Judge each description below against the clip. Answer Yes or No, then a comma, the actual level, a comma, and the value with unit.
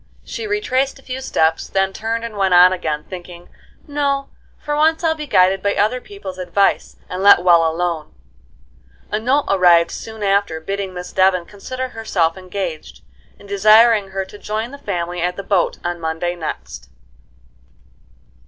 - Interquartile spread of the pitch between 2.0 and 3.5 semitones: No, average, 4.6 semitones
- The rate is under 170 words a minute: Yes, average, 160 wpm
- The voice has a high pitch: Yes, high, 195 Hz